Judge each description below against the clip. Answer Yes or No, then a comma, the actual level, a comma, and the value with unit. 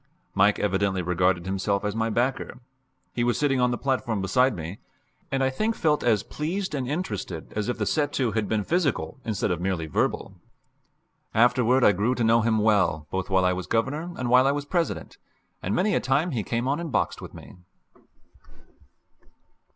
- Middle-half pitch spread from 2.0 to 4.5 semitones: No, wide, 5.4 semitones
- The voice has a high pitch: No, low, 115 Hz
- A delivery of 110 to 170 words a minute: No, average, 190 wpm